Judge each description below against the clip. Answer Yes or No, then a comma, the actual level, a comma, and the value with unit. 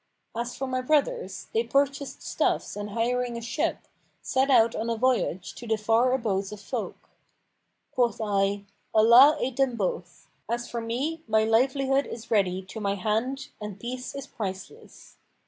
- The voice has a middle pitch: No, high, 235 Hz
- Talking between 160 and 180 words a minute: Yes, average, 165 wpm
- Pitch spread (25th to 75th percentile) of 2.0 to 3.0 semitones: No, average, 3.8 semitones